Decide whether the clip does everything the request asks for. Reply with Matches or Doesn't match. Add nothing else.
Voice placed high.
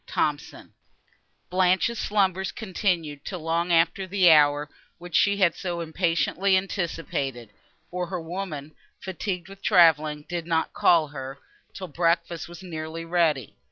Doesn't match